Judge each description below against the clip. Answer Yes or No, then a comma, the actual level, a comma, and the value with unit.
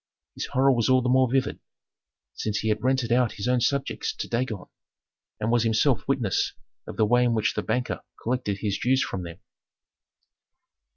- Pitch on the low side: Yes, low, 120 Hz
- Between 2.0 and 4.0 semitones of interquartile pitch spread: Yes, average, 2.9 semitones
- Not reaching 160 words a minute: No, average, 180 wpm